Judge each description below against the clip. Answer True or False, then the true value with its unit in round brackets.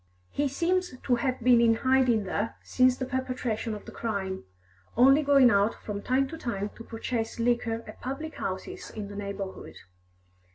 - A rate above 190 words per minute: False (170 wpm)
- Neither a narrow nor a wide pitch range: True (3.7 semitones)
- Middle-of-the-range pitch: False (240 Hz)